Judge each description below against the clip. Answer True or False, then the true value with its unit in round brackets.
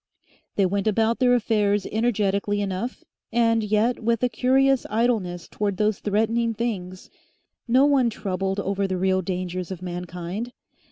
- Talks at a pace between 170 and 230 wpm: False (145 wpm)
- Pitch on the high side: True (210 Hz)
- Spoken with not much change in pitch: False (3.7 semitones)